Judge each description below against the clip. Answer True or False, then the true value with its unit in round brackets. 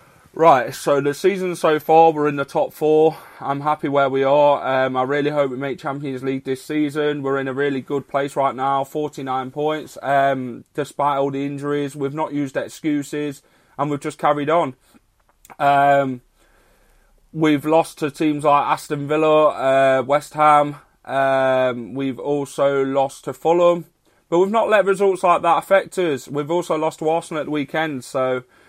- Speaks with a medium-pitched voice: True (145 Hz)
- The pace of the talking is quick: False (180 wpm)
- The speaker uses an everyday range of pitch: False (2.2 semitones)